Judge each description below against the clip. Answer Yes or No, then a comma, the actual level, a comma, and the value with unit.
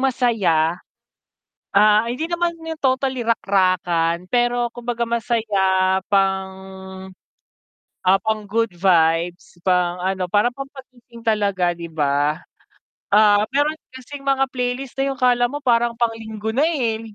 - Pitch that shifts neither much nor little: Yes, average, 4.9 semitones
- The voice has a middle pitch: No, high, 225 Hz